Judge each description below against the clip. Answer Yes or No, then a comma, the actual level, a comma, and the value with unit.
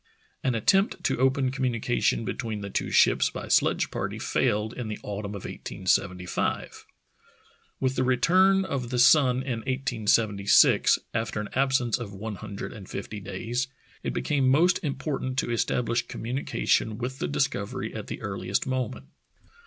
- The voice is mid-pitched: No, low, 120 Hz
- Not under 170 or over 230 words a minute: No, average, 155 wpm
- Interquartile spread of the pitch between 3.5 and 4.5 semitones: Yes, average, 3.8 semitones